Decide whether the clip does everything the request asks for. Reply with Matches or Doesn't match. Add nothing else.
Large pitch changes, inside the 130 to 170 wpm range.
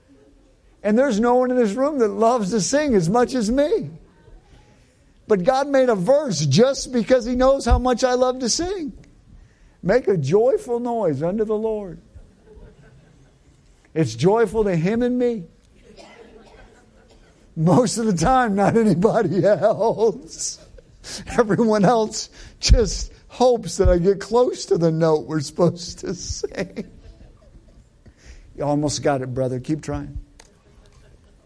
Matches